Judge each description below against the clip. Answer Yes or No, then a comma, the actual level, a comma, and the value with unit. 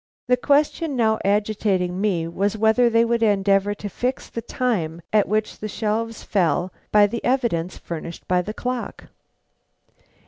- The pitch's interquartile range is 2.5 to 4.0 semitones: Yes, average, 3.5 semitones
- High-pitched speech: Yes, high, 210 Hz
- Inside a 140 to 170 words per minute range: Yes, average, 150 wpm